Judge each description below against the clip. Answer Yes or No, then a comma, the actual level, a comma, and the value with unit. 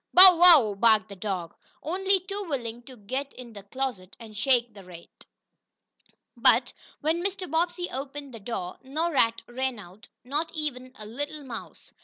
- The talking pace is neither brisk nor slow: Yes, average, 165 wpm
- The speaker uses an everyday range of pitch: No, wide, 6.4 semitones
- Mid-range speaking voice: No, very high, 255 Hz